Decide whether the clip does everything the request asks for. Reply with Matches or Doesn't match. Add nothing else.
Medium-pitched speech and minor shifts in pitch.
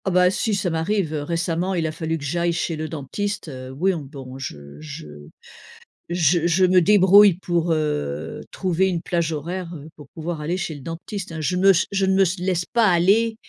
Doesn't match